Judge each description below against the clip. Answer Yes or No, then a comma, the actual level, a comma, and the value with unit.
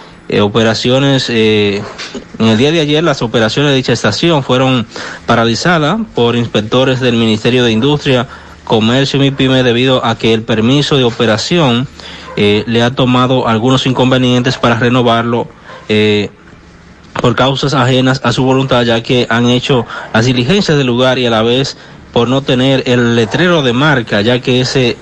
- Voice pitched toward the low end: Yes, low, 125 Hz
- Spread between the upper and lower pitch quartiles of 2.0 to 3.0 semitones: Yes, narrow, 2.4 semitones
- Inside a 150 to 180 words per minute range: Yes, average, 165 wpm